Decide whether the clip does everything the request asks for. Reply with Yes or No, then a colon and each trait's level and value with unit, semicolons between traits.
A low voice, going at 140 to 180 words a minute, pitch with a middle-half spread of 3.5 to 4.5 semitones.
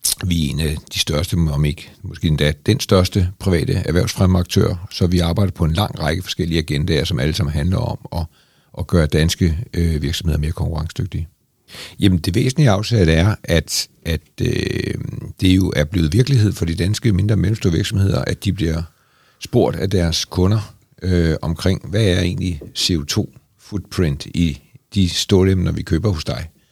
Yes: very low, 90 Hz; average, 175 wpm; average, 4.0 semitones